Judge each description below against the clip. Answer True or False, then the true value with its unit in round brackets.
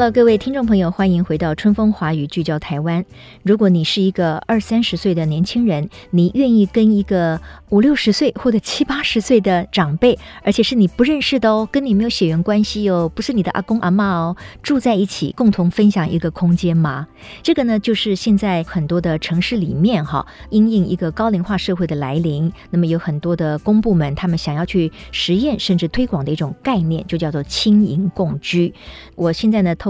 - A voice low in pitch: False (190 Hz)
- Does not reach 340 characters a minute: True (310 characters per minute)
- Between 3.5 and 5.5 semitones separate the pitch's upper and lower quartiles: True (4.5 semitones)